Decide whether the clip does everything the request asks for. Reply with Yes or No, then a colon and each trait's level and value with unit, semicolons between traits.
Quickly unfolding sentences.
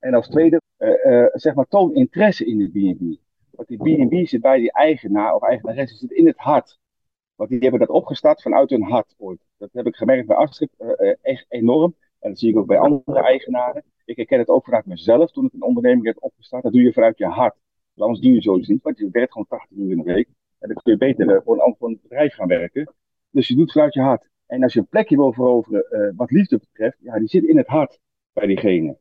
Yes: fast, 255 wpm